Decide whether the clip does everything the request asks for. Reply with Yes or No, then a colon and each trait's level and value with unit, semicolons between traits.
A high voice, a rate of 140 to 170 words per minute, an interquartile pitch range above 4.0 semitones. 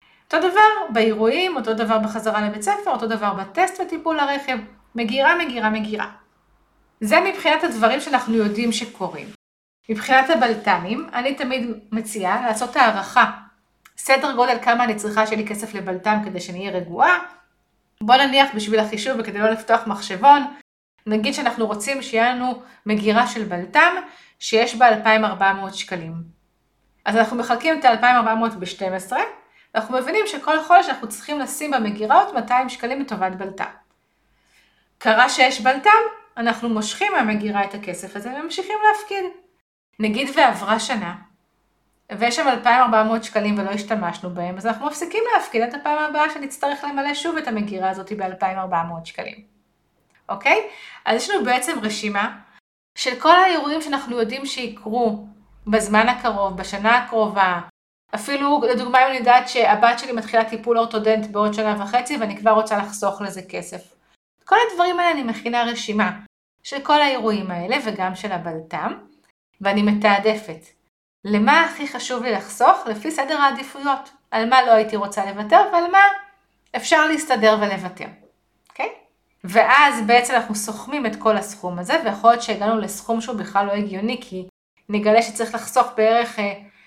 Yes: high, 230 Hz; average, 145 wpm; average, 4.4 semitones